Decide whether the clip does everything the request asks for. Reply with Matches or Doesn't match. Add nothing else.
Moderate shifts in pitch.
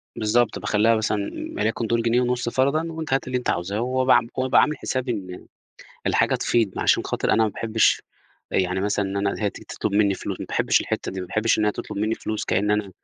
Matches